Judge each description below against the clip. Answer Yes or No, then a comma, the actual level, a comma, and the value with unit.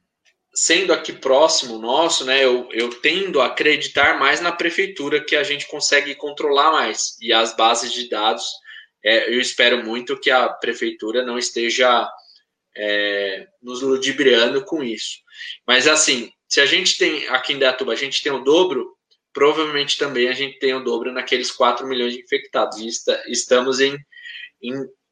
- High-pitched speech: No, medium, 140 Hz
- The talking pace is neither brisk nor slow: Yes, average, 165 wpm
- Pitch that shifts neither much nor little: No, wide, 7.2 semitones